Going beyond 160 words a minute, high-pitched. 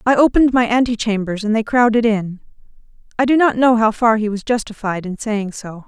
Yes: fast, 205 wpm; high, 225 Hz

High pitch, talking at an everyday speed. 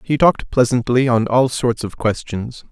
No: low, 120 Hz; average, 175 wpm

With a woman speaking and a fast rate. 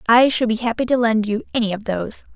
Yes: female; fast, 255 wpm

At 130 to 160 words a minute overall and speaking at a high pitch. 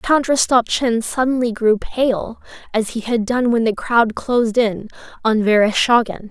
Yes: average, 150 wpm; high, 230 Hz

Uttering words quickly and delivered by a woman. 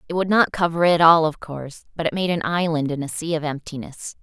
Yes: fast, 255 wpm; female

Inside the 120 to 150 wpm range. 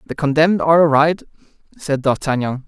Yes: slow, 135 wpm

